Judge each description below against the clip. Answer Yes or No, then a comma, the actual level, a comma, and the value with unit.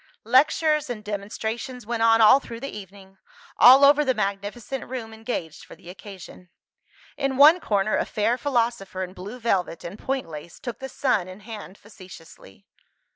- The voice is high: Yes, high, 220 Hz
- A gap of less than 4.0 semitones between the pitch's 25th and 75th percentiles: No, average, 4.7 semitones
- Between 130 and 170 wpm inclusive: Yes, average, 165 wpm